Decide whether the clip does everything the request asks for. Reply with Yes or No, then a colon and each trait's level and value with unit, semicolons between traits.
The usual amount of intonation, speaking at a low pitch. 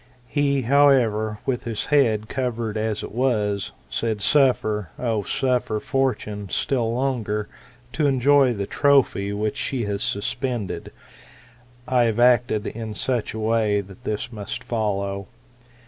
Yes: average, 3.5 semitones; low, 115 Hz